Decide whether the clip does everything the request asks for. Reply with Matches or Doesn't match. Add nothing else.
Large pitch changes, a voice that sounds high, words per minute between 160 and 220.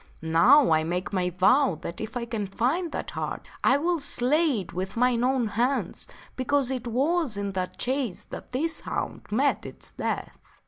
Matches